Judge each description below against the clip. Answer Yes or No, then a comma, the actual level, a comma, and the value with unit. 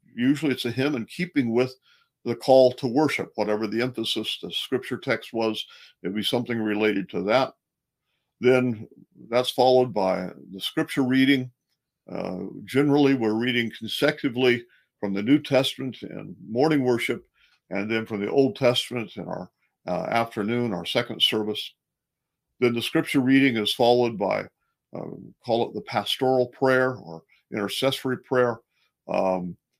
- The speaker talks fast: No, average, 145 wpm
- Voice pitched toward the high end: No, low, 125 Hz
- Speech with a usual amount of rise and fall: Yes, average, 3.5 semitones